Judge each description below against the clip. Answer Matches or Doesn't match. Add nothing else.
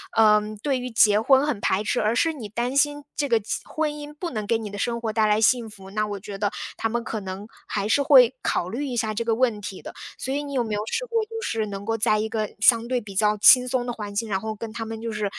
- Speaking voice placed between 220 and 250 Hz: Matches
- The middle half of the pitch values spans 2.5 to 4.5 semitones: Matches